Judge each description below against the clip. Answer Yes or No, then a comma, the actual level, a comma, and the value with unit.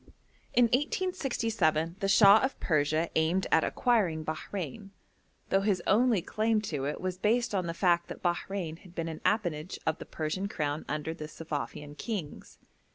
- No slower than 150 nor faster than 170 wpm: Yes, average, 160 wpm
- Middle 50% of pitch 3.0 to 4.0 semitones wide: No, average, 5.2 semitones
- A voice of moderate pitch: Yes, medium, 180 Hz